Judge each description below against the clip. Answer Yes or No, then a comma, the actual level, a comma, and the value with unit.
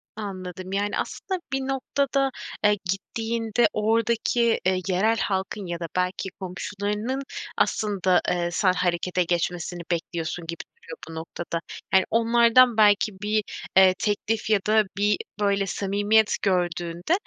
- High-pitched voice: Yes, high, 205 Hz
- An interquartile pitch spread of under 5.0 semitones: Yes, average, 3.5 semitones